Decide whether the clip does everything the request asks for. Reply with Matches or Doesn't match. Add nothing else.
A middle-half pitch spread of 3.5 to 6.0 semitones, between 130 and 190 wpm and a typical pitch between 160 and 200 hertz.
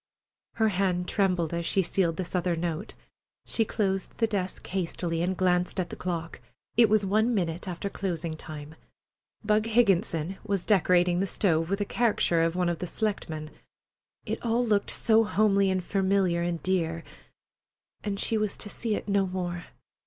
Doesn't match